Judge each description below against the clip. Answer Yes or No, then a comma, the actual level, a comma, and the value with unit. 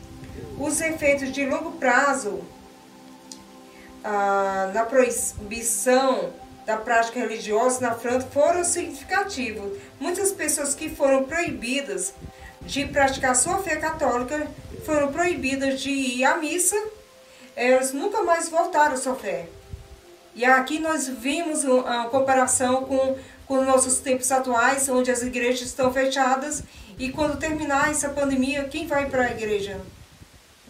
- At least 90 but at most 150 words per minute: Yes, average, 125 wpm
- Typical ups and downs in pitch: Yes, average, 3.3 semitones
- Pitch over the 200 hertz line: Yes, very high, 265 Hz